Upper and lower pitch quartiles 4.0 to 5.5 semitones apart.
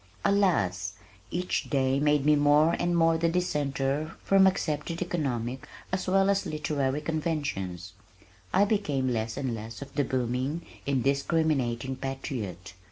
Yes: average, 4.5 semitones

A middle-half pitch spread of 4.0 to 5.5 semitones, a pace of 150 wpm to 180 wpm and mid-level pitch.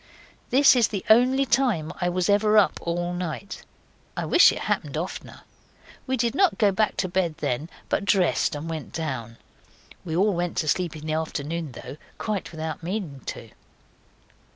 Yes: average, 5.1 semitones; average, 175 wpm; medium, 175 Hz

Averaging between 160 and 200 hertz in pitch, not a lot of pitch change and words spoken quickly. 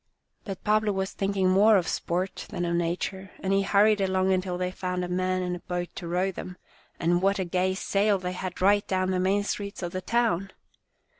Yes: medium, 185 Hz; narrow, 1.5 semitones; fast, 215 wpm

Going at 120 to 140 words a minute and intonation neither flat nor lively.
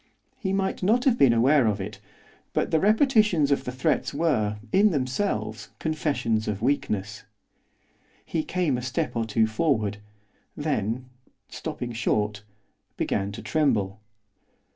No: slow, 135 wpm; wide, 7.0 semitones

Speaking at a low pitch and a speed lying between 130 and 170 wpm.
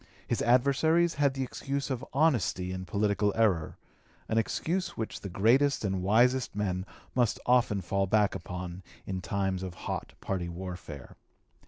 Yes: low, 105 Hz; average, 150 wpm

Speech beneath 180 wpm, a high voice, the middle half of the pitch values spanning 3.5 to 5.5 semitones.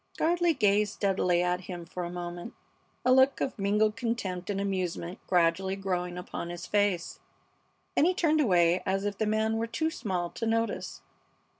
Yes: average, 170 wpm; high, 195 Hz; average, 4.2 semitones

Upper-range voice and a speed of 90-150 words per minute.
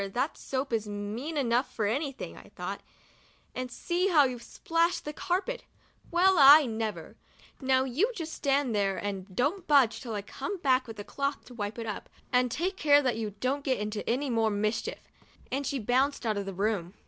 No: very high, 255 Hz; average, 200 wpm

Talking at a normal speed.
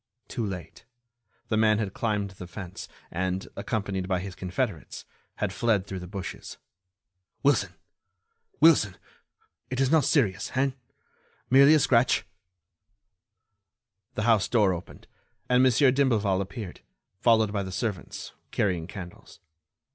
No: slow, 125 wpm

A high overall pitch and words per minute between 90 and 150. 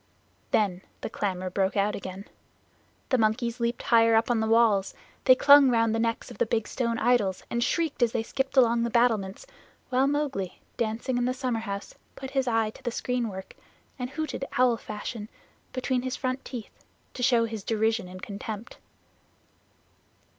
No: high, 230 Hz; average, 170 wpm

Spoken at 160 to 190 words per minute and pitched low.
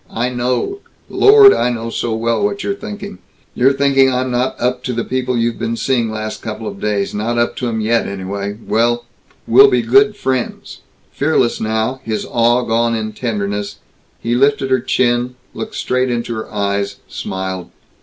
Yes: average, 175 wpm; low, 120 Hz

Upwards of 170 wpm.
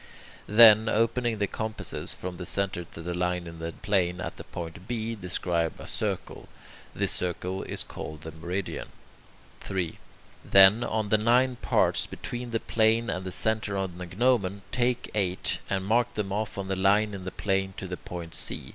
Yes: average, 180 wpm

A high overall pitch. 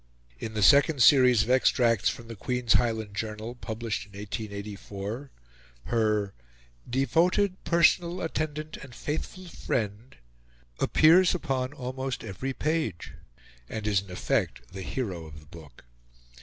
No: low, 120 Hz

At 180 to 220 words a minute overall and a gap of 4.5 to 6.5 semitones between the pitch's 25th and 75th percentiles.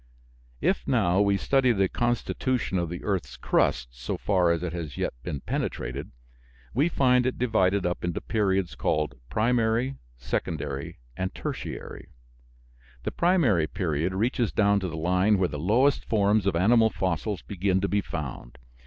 No: average, 155 wpm; average, 4.8 semitones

